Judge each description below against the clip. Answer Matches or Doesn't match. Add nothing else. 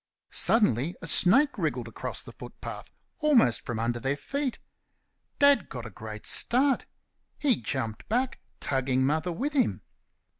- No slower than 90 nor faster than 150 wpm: Matches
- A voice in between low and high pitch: Matches